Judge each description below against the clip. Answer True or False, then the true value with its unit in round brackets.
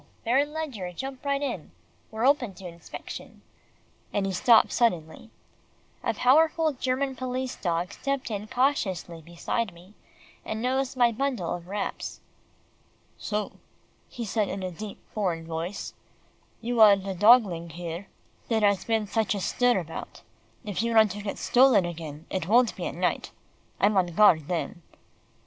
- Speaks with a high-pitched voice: True (210 Hz)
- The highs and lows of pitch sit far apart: True (5.8 semitones)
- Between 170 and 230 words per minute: False (150 wpm)